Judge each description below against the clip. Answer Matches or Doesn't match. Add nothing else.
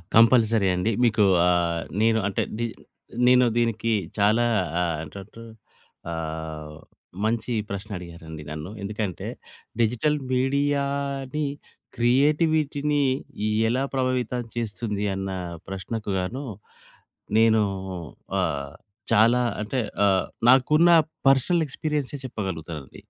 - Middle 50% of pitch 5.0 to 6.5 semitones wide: Matches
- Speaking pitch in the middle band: Doesn't match